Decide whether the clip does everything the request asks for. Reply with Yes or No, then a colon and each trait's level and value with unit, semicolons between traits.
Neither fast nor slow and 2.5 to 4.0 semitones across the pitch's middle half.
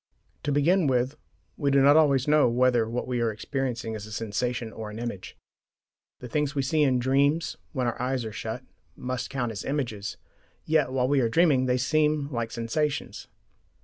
Yes: average, 185 wpm; average, 3.5 semitones